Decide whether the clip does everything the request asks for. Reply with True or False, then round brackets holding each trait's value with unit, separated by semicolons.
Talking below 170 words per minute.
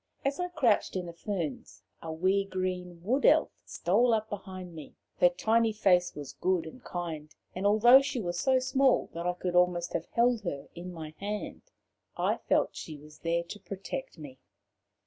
False (185 wpm)